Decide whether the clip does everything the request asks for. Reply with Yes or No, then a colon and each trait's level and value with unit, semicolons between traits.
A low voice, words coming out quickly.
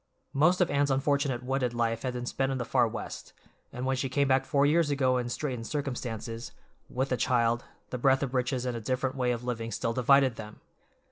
Yes: low, 130 Hz; fast, 215 wpm